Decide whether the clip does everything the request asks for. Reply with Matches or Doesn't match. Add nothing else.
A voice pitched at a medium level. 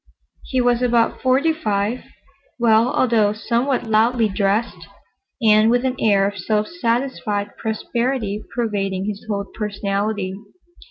Doesn't match